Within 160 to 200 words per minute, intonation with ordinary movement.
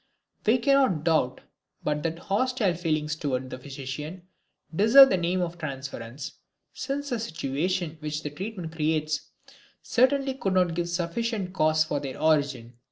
No: average, 150 wpm; average, 4.8 semitones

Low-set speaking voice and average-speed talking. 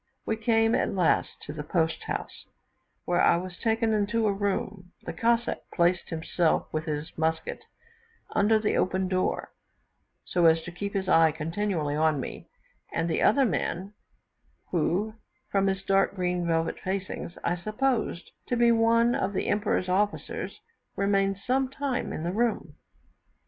No: high, 190 Hz; average, 155 wpm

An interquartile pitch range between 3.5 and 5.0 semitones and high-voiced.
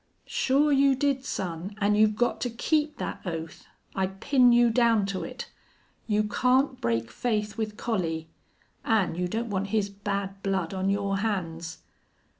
Yes: average, 4.1 semitones; high, 210 Hz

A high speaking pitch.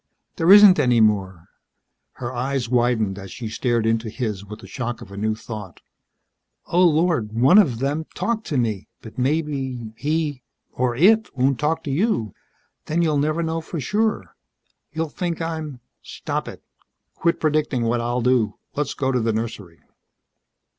No: low, 130 Hz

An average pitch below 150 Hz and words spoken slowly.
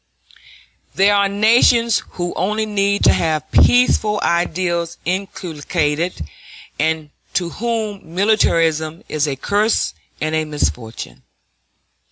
No: medium, 175 Hz; slow, 105 wpm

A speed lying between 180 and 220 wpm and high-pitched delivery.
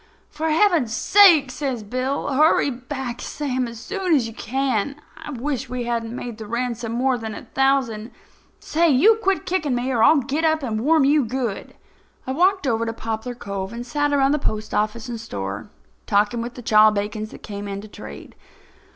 Yes: average, 185 wpm; very high, 250 Hz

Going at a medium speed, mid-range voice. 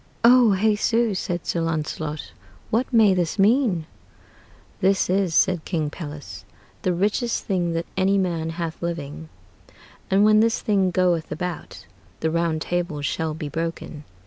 Yes: average, 145 wpm; medium, 175 Hz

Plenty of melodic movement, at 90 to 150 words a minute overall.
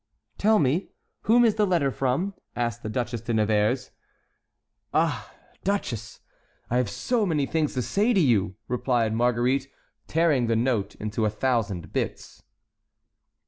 Yes: wide, 6.3 semitones; average, 140 wpm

